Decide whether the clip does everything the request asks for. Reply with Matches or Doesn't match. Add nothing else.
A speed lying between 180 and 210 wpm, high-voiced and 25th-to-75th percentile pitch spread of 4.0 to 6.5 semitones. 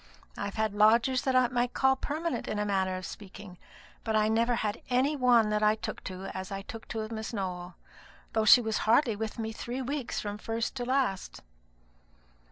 Doesn't match